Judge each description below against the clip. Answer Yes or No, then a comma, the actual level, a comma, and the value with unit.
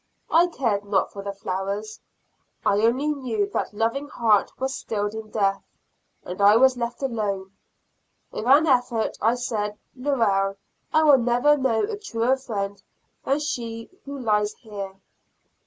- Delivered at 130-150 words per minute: Yes, average, 145 wpm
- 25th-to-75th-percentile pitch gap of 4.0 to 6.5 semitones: Yes, average, 4.5 semitones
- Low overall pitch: No, high, 230 Hz